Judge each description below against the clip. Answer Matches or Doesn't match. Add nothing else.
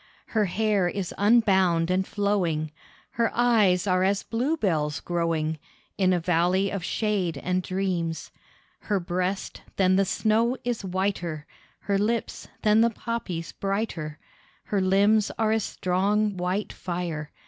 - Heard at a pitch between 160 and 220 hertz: Matches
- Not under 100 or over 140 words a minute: Matches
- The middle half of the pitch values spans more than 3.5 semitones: Doesn't match